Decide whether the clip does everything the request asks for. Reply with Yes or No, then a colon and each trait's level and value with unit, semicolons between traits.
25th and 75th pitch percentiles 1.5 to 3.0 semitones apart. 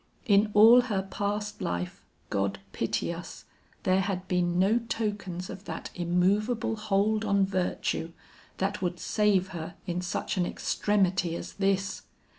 Yes: average, 2.7 semitones